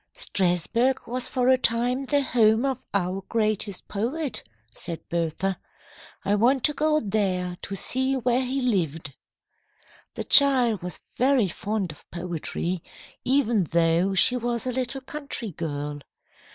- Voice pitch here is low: No, high, 225 Hz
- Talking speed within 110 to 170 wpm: Yes, average, 140 wpm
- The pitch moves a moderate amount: No, wide, 6.1 semitones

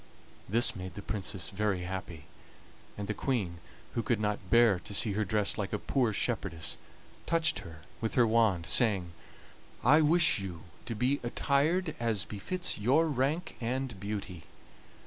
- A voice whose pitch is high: No, low, 110 Hz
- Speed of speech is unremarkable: Yes, average, 155 wpm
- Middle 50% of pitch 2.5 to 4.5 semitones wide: No, average, 5.0 semitones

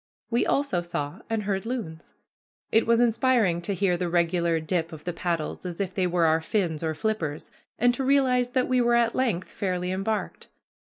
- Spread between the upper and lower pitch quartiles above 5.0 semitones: Yes, wide, 5.6 semitones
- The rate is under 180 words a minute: No, average, 195 wpm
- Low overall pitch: No, medium, 185 Hz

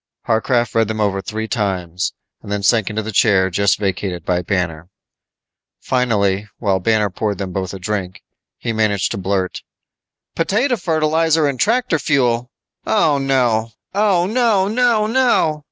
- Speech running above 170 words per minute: No, average, 145 wpm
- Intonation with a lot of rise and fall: Yes, wide, 8.2 semitones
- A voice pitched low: Yes, low, 110 Hz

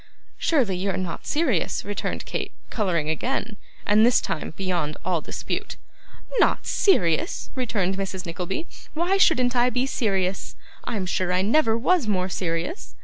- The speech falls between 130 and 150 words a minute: Yes, average, 145 wpm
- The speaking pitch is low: No, high, 200 Hz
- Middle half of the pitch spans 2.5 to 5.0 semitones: No, wide, 5.6 semitones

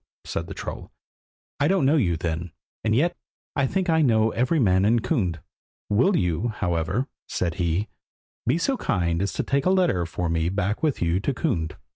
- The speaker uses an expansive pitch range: Yes, wide, 8.4 semitones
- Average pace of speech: Yes, average, 190 wpm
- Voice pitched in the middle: No, low, 105 Hz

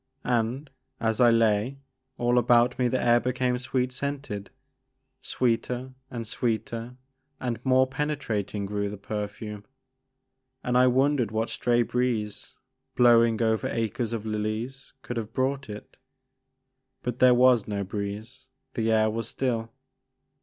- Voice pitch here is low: Yes, low, 120 Hz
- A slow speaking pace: Yes, slow, 130 wpm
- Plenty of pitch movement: No, average, 2.7 semitones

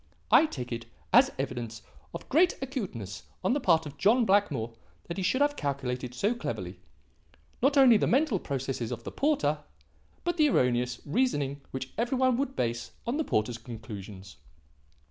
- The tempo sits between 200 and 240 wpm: No, average, 165 wpm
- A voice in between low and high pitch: Yes, medium, 150 Hz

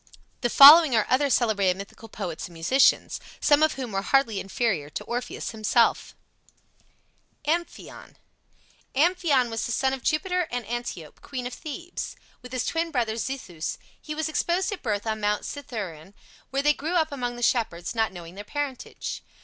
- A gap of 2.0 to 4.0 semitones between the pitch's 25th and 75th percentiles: No, wide, 5.6 semitones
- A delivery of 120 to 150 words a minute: No, average, 165 wpm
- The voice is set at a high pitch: Yes, high, 245 Hz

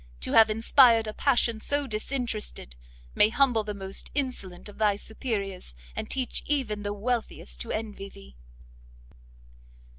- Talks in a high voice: Yes, high, 215 Hz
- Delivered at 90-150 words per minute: Yes, average, 140 wpm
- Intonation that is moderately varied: Yes, average, 3.6 semitones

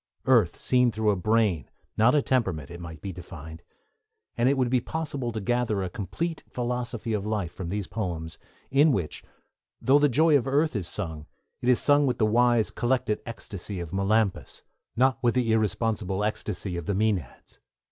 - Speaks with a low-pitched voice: Yes, low, 110 Hz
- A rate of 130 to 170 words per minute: No, average, 180 wpm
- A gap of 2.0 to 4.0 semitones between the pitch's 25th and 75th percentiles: No, average, 4.8 semitones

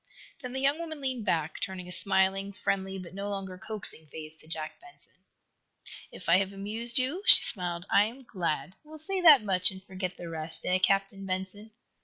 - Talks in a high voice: Yes, high, 195 Hz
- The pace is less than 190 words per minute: No, average, 200 wpm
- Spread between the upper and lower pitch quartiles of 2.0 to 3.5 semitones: No, average, 4.2 semitones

